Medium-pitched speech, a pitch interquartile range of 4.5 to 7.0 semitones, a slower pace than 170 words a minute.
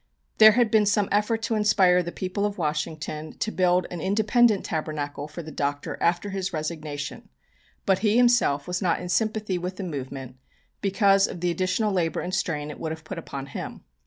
No: medium, 180 Hz; average, 4.8 semitones; average, 190 wpm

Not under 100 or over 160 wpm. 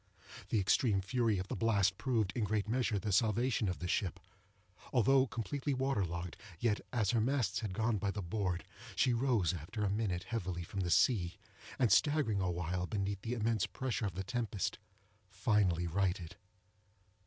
No: average, 175 wpm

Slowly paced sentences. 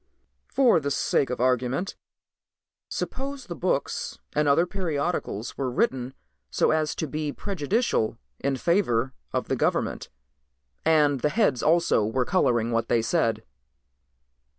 Yes: slow, 130 wpm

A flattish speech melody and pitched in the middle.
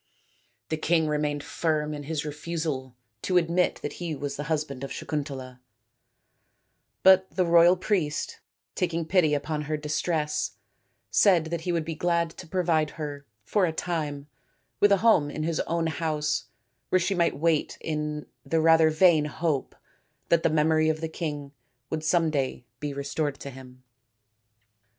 Yes: narrow, 2.3 semitones; medium, 155 Hz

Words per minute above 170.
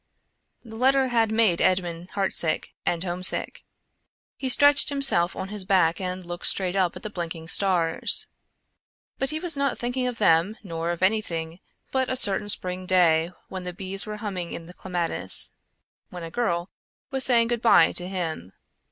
Yes: average, 180 wpm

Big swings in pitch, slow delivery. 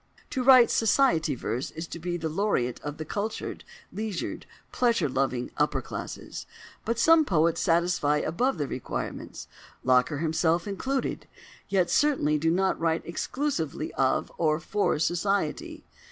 Yes: wide, 5.7 semitones; slow, 130 wpm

